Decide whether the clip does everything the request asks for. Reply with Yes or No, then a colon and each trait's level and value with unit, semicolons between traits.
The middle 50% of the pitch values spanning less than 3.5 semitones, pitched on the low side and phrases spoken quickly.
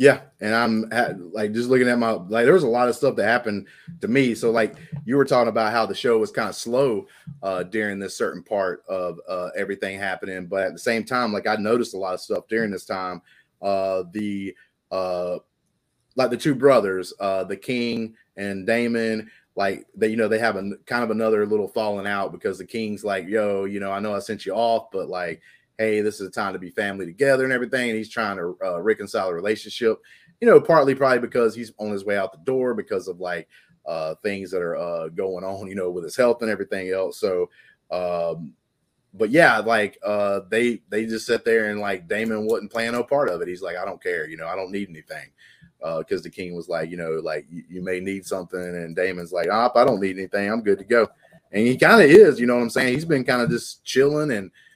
No: average, 4.3 semitones; low, 110 Hz; fast, 240 wpm